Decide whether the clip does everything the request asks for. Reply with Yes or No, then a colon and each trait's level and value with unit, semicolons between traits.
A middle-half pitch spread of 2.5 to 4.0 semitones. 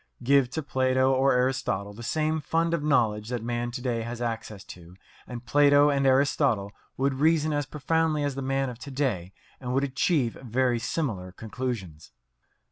Yes: average, 3.4 semitones